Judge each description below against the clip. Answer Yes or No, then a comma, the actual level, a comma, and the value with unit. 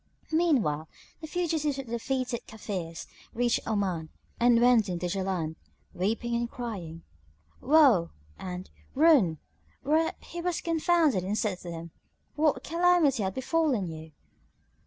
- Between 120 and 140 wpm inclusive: Yes, slow, 135 wpm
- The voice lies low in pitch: No, high, 235 Hz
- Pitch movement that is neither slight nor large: No, wide, 8.8 semitones